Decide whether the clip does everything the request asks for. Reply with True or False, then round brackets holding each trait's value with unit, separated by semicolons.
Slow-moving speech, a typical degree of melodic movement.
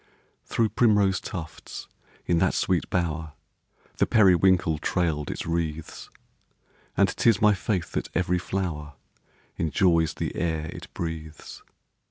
True (120 wpm; 3.0 semitones)